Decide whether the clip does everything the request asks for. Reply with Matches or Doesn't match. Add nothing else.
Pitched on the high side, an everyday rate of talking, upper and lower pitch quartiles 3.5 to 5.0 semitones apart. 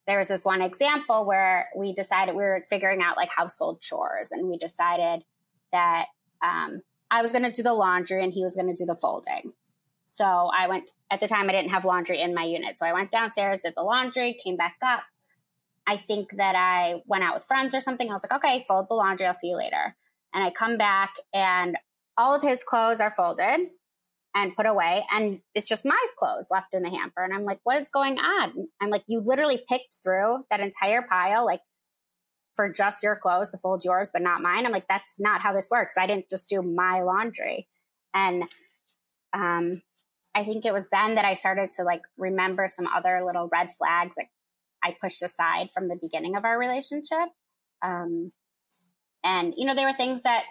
Doesn't match